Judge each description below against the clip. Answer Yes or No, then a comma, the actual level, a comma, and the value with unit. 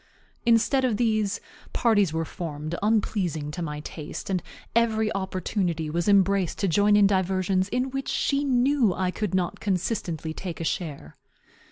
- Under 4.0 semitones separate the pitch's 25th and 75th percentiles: No, average, 4.3 semitones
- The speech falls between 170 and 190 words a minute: No, average, 155 wpm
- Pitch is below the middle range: No, high, 195 Hz